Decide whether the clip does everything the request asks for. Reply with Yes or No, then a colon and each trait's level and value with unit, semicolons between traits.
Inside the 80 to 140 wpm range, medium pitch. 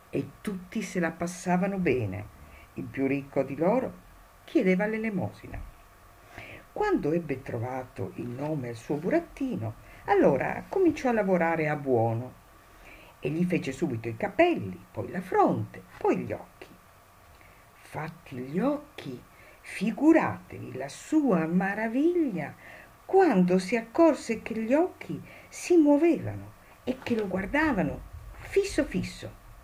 Yes: average, 120 wpm; medium, 180 Hz